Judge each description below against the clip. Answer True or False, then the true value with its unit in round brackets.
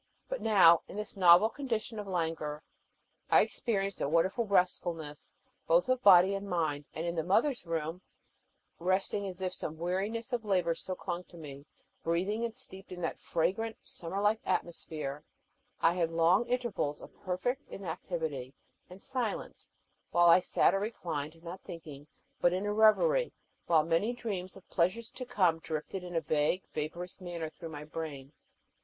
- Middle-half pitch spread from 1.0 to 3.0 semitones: False (4.1 semitones)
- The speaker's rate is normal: True (165 wpm)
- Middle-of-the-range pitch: True (180 Hz)